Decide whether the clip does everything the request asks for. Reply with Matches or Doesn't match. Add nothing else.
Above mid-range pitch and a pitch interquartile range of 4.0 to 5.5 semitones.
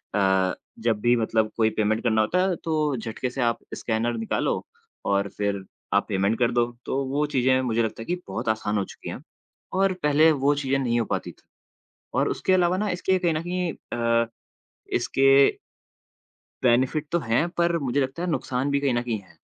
Doesn't match